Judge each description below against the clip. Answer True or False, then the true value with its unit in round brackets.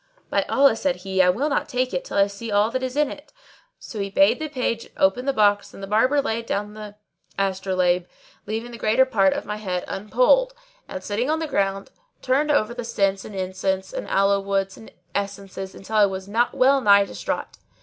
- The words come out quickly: True (210 wpm)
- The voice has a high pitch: True (210 Hz)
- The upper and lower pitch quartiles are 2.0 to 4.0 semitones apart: False (4.6 semitones)